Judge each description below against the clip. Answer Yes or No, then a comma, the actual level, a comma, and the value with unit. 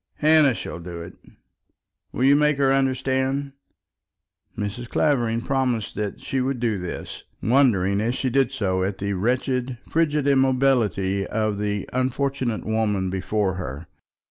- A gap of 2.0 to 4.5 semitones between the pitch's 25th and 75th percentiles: No, average, 5.0 semitones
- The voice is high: No, low, 120 Hz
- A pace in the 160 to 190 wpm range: No, average, 140 wpm